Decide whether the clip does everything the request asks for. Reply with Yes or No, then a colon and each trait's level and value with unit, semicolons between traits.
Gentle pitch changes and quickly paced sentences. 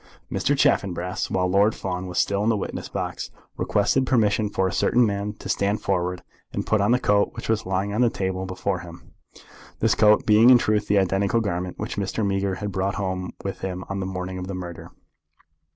Yes: narrow, 2.1 semitones; fast, 210 wpm